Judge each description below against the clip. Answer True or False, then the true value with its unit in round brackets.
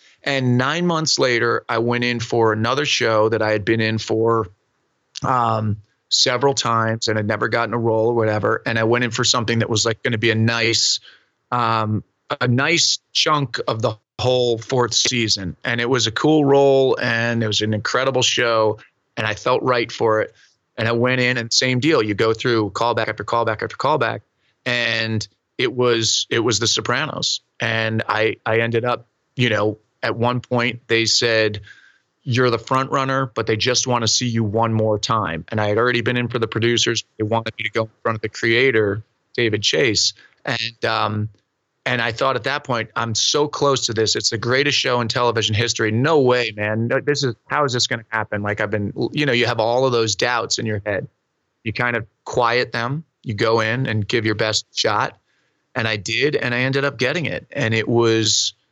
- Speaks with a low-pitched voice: True (115 Hz)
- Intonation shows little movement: True (2.1 semitones)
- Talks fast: True (210 wpm)